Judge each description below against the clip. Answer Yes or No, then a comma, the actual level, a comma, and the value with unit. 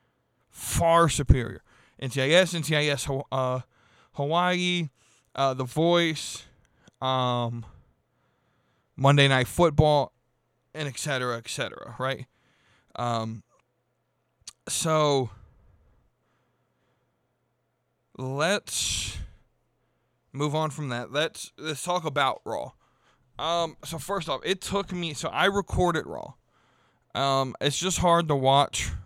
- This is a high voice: No, low, 135 Hz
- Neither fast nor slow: No, slow, 100 wpm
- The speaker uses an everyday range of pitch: Yes, average, 4.5 semitones